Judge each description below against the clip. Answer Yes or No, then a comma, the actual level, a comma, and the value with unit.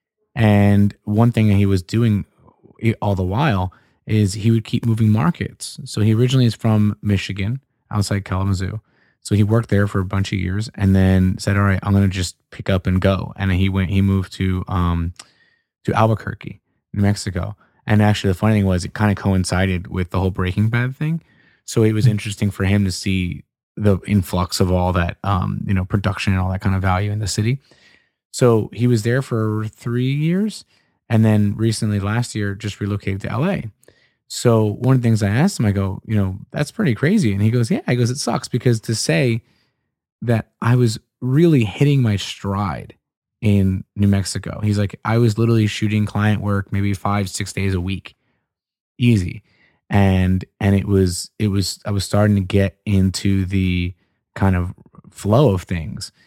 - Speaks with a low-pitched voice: Yes, low, 105 Hz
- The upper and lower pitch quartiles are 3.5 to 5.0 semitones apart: No, average, 2.9 semitones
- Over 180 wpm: Yes, average, 195 wpm